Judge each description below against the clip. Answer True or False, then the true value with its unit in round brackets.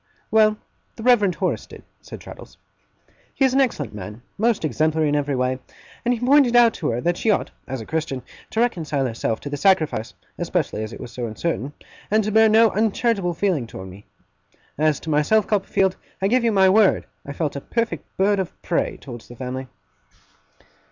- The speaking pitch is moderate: True (170 Hz)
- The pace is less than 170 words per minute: False (195 wpm)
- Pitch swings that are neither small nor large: False (8.5 semitones)